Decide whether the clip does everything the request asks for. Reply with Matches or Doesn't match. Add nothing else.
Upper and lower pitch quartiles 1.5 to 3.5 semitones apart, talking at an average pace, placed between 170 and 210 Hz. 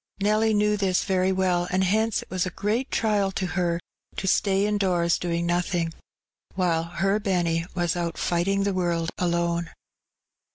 Matches